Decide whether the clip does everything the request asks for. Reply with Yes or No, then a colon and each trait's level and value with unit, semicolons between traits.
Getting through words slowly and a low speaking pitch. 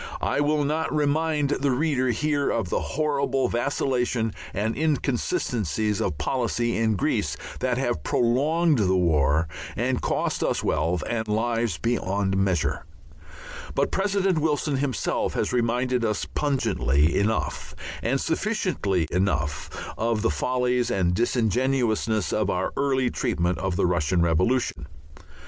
Yes: slow, 130 wpm; low, 120 Hz